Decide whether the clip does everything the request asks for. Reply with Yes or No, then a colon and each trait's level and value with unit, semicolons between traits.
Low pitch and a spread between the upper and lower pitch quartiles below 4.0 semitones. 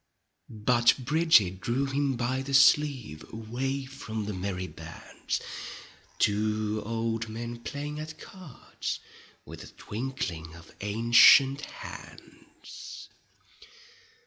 No: low, 120 Hz; average, 4.3 semitones